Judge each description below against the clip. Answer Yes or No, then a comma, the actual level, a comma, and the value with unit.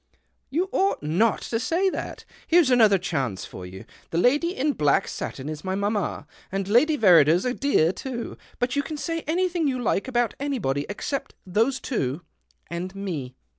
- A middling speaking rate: Yes, average, 180 wpm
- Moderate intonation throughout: No, wide, 8.7 semitones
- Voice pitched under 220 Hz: No, high, 225 Hz